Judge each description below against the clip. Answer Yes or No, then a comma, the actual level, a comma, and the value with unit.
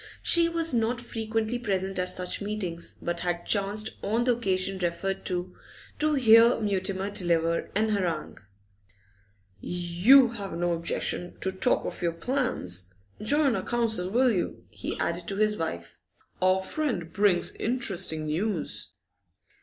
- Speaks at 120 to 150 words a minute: Yes, average, 140 wpm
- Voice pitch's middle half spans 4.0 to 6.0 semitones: Yes, average, 4.6 semitones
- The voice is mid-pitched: No, high, 195 Hz